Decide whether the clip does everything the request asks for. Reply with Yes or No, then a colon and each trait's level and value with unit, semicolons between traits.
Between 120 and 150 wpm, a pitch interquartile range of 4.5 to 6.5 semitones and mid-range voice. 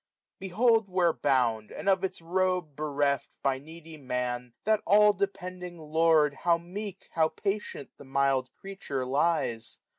Yes: average, 140 wpm; wide, 5.4 semitones; medium, 165 Hz